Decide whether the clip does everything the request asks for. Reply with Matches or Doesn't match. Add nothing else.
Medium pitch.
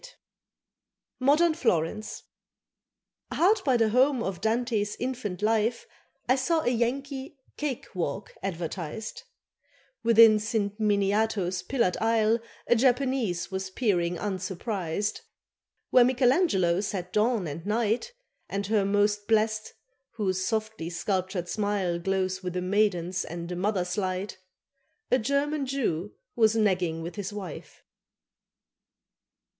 Doesn't match